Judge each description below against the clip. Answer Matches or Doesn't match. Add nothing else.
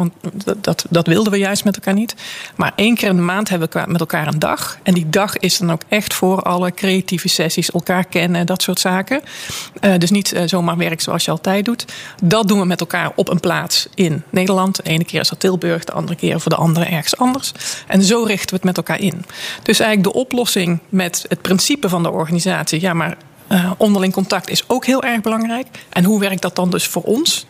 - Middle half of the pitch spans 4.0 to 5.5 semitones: Doesn't match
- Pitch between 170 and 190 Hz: Matches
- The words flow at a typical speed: Doesn't match